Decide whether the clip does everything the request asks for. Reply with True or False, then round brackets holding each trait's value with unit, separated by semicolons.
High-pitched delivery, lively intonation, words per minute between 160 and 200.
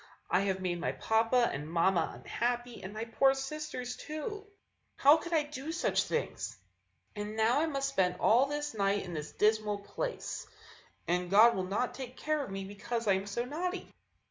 True (235 Hz; 6.0 semitones; 185 wpm)